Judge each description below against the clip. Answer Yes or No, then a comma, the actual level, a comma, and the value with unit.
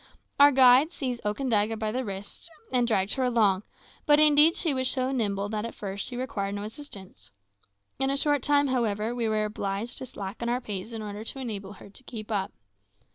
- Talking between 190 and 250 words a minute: Yes, average, 200 wpm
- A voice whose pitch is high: Yes, high, 230 Hz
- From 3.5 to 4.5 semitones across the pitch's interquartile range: Yes, average, 4.1 semitones